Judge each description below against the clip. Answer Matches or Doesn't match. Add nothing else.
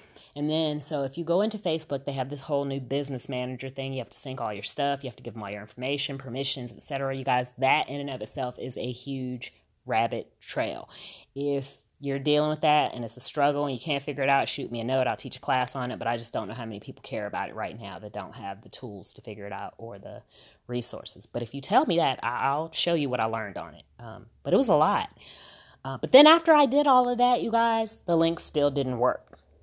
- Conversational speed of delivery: Doesn't match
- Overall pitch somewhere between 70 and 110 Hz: Doesn't match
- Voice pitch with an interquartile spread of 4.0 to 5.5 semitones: Doesn't match